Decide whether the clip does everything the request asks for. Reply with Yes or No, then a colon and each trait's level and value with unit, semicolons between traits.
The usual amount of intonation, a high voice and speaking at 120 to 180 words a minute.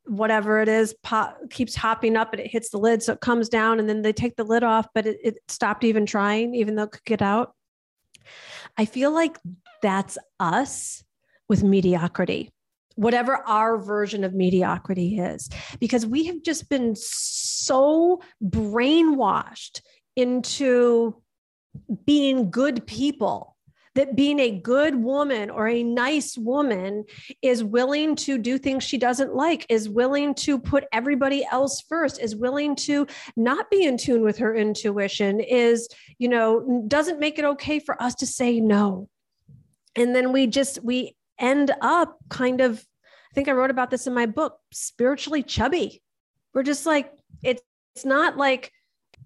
Yes: average, 4.0 semitones; high, 245 Hz; average, 160 wpm